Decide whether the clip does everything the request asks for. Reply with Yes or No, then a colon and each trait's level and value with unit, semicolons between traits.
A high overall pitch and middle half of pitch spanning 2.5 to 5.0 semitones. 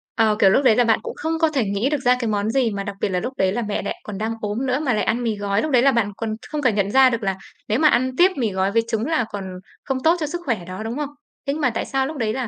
Yes: high, 230 Hz; average, 4.5 semitones